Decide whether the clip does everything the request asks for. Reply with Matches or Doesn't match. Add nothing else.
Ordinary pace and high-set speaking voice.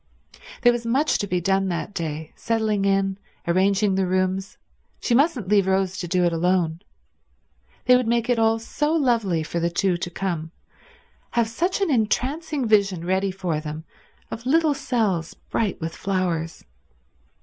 Matches